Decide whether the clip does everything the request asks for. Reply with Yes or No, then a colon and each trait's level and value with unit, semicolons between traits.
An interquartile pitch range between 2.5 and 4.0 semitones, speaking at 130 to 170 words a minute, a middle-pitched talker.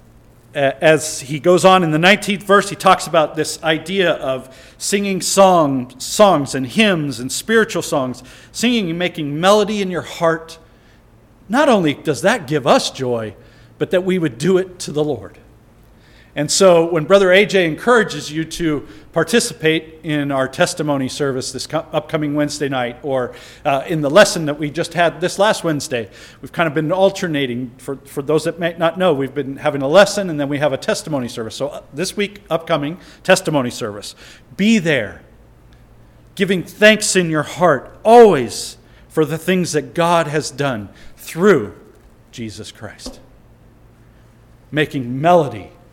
No: average, 5.2 semitones; average, 160 wpm; medium, 155 Hz